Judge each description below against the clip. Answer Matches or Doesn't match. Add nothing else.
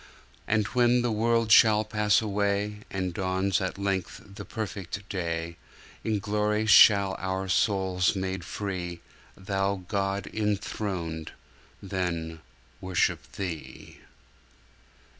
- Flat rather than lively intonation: Matches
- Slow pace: Matches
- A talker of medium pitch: Doesn't match